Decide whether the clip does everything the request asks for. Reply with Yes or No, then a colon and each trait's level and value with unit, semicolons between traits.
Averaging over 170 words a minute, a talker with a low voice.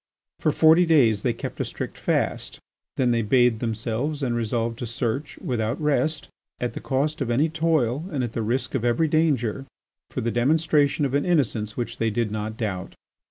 Yes: average, 190 wpm; low, 125 Hz